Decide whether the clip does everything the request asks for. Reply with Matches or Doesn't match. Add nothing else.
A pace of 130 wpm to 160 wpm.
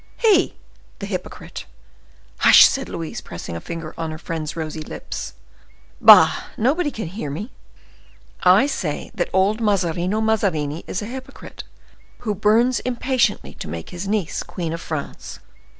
Matches